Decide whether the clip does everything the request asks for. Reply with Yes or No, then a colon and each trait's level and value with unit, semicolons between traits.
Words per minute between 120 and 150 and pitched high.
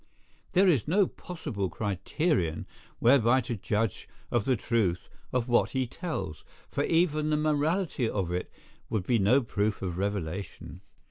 No: average, 145 wpm; low, 115 Hz